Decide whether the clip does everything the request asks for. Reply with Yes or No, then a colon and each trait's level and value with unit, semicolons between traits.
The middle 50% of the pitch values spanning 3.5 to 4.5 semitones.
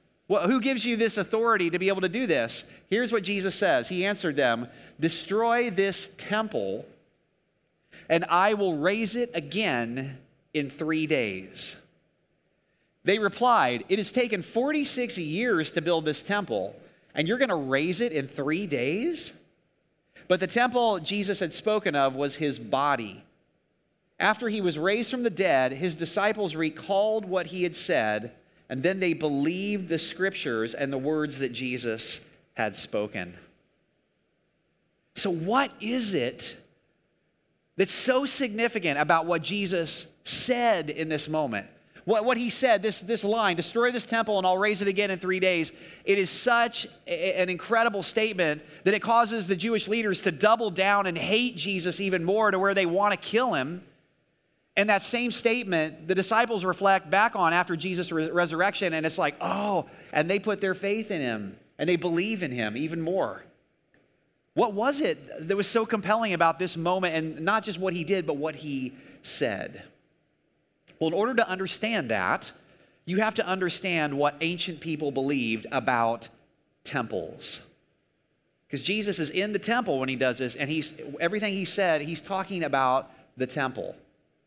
No: average, 5.1 semitones